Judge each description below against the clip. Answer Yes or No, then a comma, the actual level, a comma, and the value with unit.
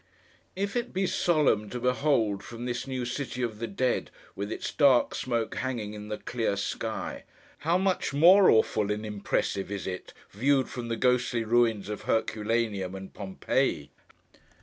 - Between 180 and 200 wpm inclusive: No, average, 160 wpm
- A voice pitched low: Yes, low, 115 Hz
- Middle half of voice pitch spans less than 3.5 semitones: No, average, 3.8 semitones